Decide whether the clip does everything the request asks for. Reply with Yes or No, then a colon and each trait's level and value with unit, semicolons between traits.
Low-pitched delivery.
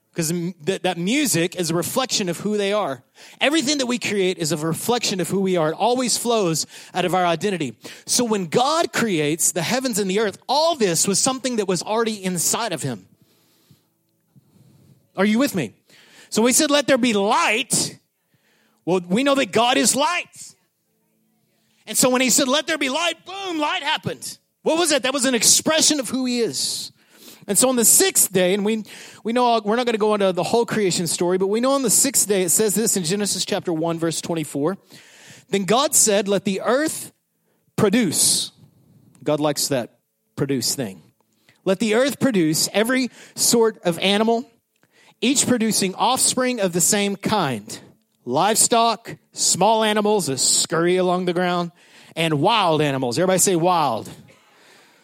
No: high, 205 Hz